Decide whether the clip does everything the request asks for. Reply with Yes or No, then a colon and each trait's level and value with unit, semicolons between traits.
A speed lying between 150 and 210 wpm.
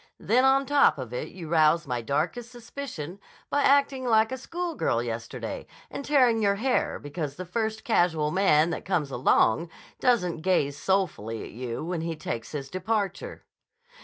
Yes: average, 165 wpm